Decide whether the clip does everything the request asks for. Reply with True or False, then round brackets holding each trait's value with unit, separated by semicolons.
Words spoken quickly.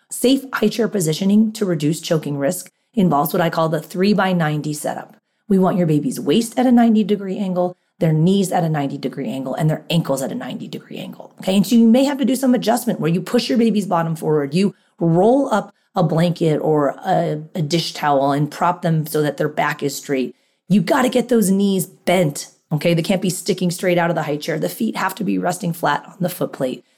True (240 wpm)